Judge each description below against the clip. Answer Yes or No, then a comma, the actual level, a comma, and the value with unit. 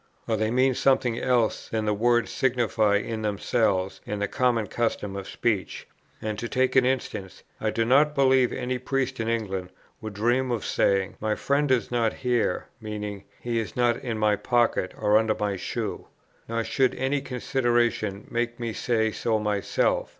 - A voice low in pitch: Yes, low, 115 Hz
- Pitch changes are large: No, average, 2.8 semitones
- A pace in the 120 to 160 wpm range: No, average, 175 wpm